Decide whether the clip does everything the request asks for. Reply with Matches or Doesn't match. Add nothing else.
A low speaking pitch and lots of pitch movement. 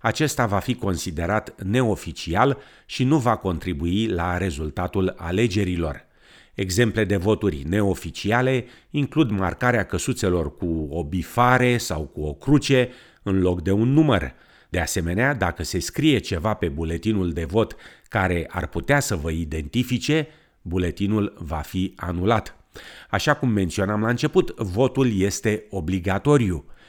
Matches